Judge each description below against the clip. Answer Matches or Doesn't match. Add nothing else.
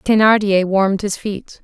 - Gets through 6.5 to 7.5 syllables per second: Doesn't match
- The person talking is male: Doesn't match